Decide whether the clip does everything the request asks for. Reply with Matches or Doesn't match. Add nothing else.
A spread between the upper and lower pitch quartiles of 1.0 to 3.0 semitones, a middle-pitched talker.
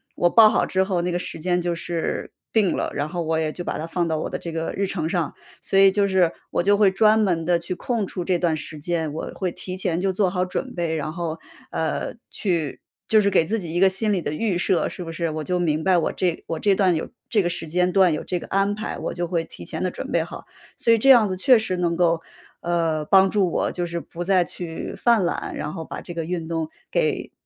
Matches